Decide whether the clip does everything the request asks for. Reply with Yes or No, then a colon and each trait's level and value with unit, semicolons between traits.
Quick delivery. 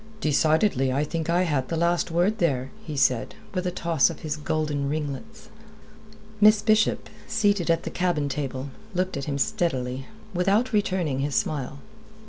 No: average, 160 wpm